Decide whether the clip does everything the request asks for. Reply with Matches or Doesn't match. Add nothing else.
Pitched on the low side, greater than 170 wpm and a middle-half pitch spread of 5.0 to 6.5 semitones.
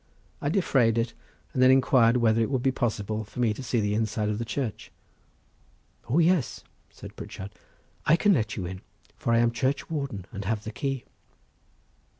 Doesn't match